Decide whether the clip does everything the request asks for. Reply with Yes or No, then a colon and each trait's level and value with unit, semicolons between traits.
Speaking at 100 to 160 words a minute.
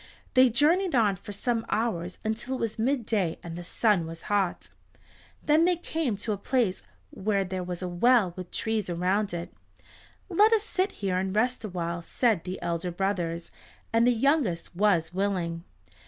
No: average, 170 wpm